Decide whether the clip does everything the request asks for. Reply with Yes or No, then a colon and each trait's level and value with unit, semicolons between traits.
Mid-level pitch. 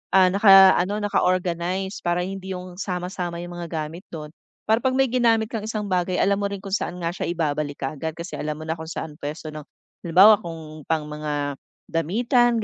Yes: medium, 180 Hz